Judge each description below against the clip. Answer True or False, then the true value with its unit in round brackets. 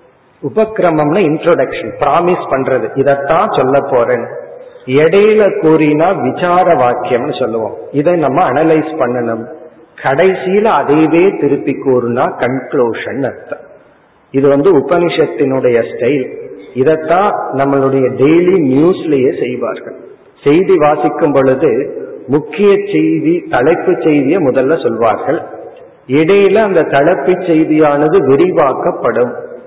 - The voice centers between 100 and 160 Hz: False (175 Hz)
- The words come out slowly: False (90 wpm)